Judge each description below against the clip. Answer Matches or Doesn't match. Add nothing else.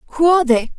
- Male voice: Doesn't match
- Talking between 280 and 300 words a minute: Doesn't match